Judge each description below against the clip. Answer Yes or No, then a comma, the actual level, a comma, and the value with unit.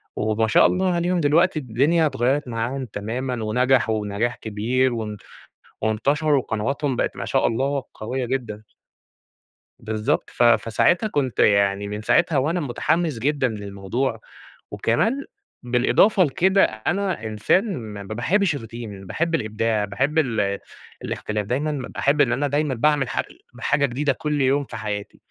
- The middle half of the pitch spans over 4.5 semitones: Yes, wide, 5.4 semitones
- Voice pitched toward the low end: Yes, low, 125 Hz